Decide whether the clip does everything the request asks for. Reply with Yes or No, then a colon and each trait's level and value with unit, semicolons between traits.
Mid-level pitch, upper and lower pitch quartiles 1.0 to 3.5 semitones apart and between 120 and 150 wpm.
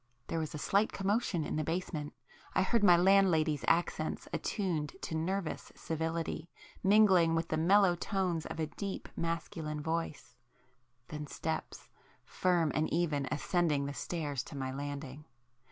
Yes: medium, 160 Hz; average, 3.2 semitones; average, 145 wpm